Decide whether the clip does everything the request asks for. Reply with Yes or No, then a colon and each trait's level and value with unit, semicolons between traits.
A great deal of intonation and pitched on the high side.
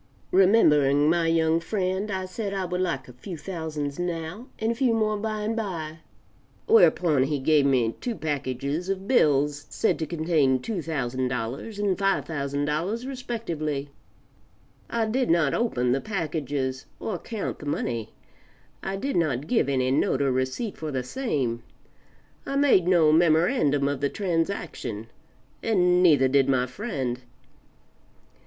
No: wide, 6.1 semitones; medium, 160 Hz